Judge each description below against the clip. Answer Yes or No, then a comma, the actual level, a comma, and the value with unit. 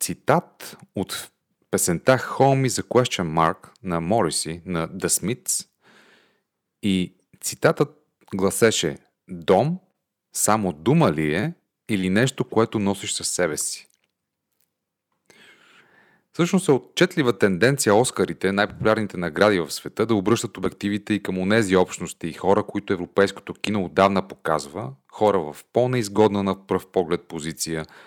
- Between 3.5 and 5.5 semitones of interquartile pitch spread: Yes, average, 4.7 semitones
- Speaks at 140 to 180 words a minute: No, average, 125 wpm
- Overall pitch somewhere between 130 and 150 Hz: No, low, 100 Hz